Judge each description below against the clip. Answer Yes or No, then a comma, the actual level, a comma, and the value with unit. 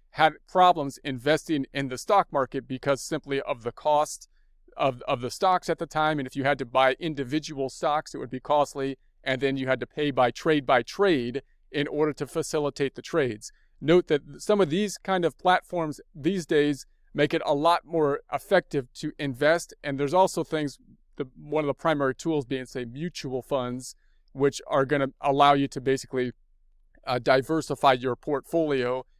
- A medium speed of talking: Yes, average, 185 wpm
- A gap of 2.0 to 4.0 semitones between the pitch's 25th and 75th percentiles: Yes, average, 2.8 semitones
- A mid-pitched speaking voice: Yes, medium, 145 Hz